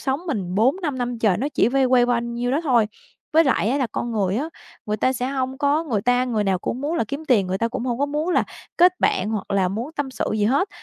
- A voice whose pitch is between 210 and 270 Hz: Yes, very high, 250 Hz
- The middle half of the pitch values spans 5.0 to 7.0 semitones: No, average, 4.4 semitones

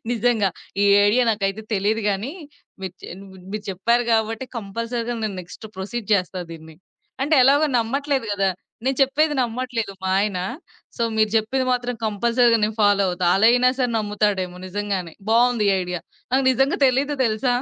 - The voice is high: Yes, high, 220 Hz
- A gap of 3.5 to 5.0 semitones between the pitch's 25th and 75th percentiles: Yes, average, 3.8 semitones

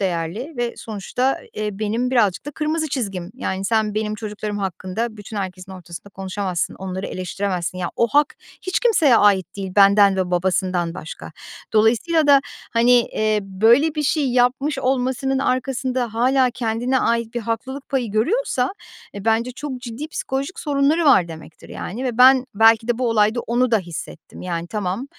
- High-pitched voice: Yes, high, 225 Hz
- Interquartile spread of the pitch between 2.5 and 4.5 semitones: No, average, 5.0 semitones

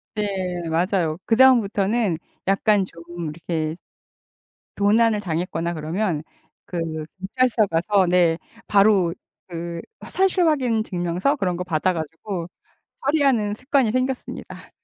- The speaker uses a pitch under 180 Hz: No, high, 190 Hz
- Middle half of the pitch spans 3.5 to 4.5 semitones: No, average, 4.9 semitones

